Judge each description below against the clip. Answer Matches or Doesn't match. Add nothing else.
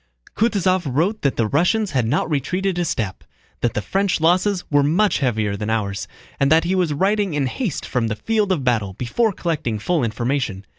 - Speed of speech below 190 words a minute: Doesn't match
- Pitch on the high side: Doesn't match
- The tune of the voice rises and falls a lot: Matches